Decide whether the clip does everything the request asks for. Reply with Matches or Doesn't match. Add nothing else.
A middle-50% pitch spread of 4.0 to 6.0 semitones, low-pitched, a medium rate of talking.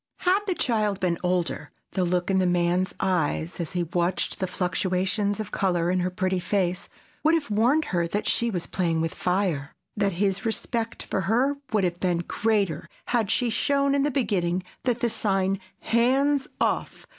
Doesn't match